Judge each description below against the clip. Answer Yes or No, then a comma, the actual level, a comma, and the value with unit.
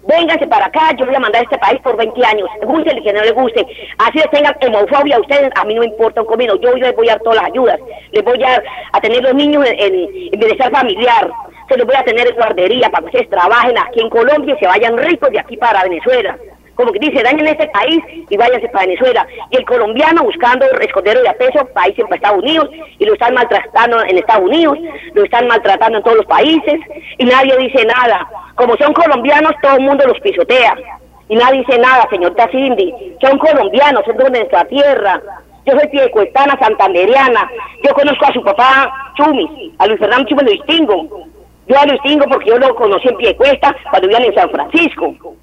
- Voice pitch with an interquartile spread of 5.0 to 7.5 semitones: Yes, wide, 5.4 semitones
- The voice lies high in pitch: Yes, very high, 275 Hz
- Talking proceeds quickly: Yes, fast, 215 wpm